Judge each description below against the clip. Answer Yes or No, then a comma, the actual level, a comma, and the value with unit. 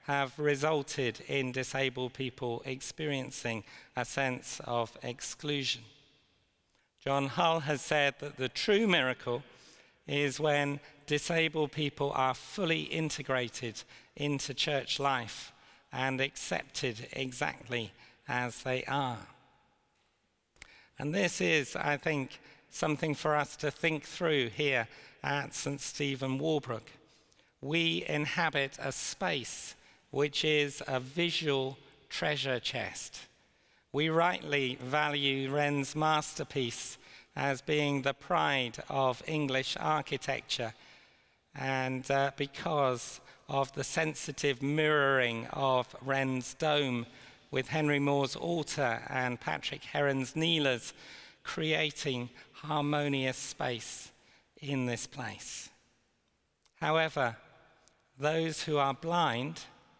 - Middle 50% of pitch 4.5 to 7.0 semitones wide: No, narrow, 2.5 semitones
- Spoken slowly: Yes, slow, 100 wpm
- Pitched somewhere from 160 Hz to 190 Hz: No, medium, 140 Hz